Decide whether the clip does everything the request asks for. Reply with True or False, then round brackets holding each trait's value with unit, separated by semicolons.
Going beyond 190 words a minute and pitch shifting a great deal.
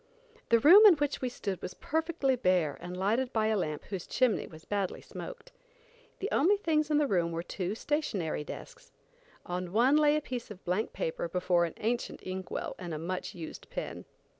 True (200 wpm; 8.5 semitones)